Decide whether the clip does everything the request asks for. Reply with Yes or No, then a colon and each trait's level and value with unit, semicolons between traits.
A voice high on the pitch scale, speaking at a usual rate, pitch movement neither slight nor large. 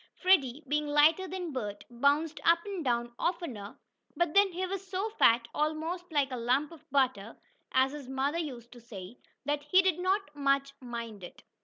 No: very high, 290 Hz; average, 180 wpm; wide, 5.8 semitones